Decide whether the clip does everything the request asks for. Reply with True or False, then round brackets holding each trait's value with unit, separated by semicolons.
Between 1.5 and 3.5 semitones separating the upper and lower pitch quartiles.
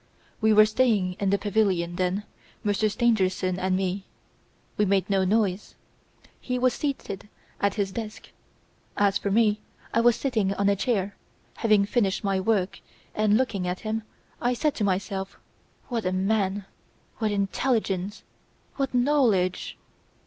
True (2.6 semitones)